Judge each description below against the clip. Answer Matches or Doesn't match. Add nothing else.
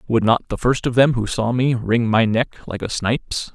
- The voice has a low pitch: Matches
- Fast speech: Matches